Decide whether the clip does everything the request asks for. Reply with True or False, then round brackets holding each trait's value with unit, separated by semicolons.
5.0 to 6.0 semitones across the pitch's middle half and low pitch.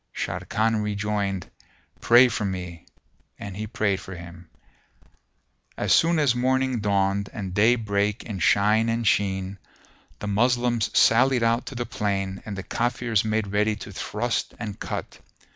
False (3.0 semitones; 105 Hz)